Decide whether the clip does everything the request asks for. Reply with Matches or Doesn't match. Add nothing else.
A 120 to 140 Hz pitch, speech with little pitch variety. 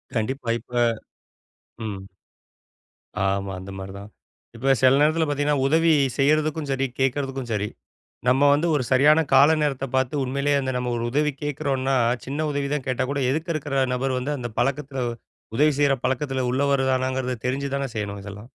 Matches